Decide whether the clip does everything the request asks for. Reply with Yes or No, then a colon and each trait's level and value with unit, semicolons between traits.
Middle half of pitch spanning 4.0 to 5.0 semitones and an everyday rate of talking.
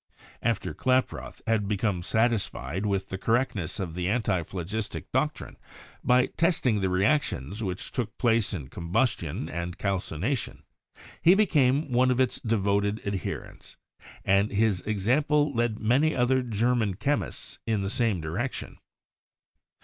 No: average, 4.7 semitones; slow, 125 wpm